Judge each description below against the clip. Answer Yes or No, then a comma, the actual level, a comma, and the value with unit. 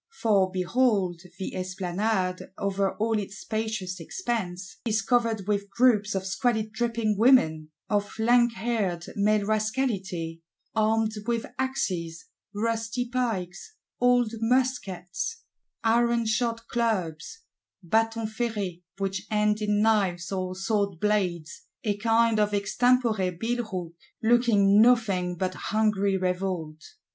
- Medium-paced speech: No, slow, 105 wpm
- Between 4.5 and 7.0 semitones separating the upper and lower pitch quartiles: No, average, 3.5 semitones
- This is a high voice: Yes, high, 210 Hz